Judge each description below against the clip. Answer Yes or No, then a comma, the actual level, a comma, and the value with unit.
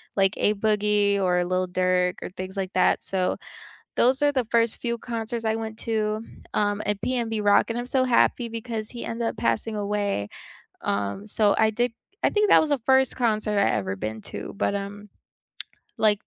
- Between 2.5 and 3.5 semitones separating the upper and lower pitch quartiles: Yes, average, 3.0 semitones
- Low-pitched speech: No, high, 210 Hz